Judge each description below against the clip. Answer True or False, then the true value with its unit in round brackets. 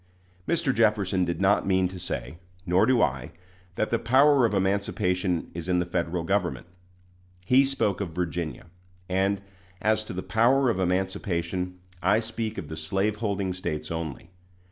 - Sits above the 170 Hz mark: False (95 Hz)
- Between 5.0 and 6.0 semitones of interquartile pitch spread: False (3.5 semitones)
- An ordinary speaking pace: True (155 wpm)